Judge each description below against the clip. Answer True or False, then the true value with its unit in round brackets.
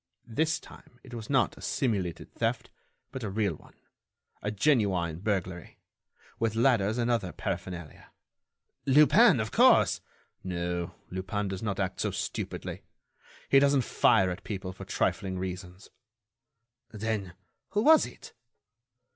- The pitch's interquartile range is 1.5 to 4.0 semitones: False (4.5 semitones)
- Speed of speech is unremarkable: False (130 wpm)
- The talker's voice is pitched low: True (105 Hz)